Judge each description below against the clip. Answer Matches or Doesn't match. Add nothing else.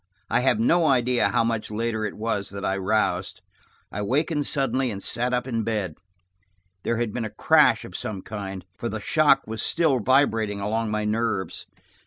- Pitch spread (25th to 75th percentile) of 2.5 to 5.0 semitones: Matches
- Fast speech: Doesn't match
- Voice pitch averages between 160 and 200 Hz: Doesn't match